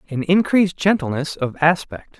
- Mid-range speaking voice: Yes, medium, 160 Hz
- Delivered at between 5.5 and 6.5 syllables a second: No, 5.0 syllables/s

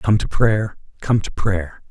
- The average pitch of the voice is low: Yes, low, 100 Hz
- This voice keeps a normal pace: Yes, average, 190 wpm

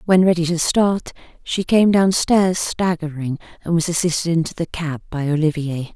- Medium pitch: Yes, medium, 170 Hz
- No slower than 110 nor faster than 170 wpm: Yes, average, 160 wpm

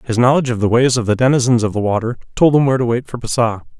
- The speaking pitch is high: No, low, 120 Hz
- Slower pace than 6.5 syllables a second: No, 7.4 syllables/s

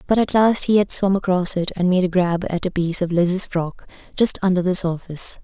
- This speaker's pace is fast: Yes, fast, 245 wpm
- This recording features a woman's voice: Yes, female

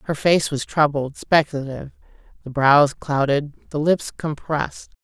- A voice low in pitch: No, medium, 145 Hz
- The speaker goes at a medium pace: No, slow, 130 wpm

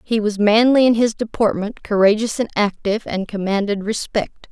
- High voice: Yes, high, 215 Hz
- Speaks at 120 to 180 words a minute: Yes, average, 160 wpm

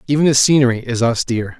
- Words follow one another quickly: No, average, 190 wpm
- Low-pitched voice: Yes, low, 125 Hz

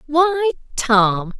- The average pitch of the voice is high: Yes, very high, 275 Hz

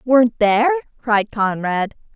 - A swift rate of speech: No, slow, 110 wpm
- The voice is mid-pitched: No, high, 230 Hz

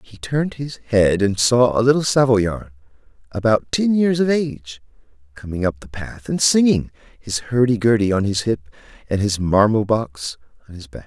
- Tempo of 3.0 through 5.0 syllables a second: Yes, 4.8 syllables/s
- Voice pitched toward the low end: Yes, low, 110 Hz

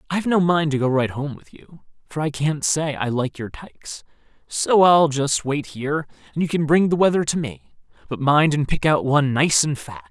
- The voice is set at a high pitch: No, medium, 145 Hz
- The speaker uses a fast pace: Yes, fast, 230 wpm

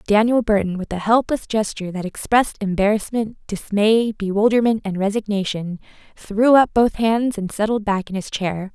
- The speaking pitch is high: Yes, high, 210 Hz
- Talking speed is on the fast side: No, average, 160 wpm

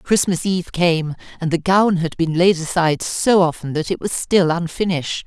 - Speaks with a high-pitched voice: No, medium, 170 Hz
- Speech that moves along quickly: No, average, 195 wpm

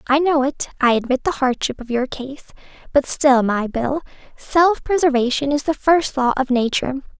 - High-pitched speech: Yes, very high, 275 Hz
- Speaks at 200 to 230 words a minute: No, average, 185 wpm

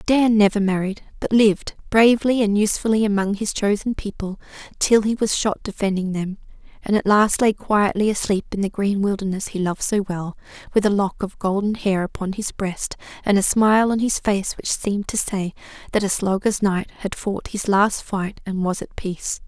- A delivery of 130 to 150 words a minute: No, average, 195 wpm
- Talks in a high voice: Yes, high, 205 Hz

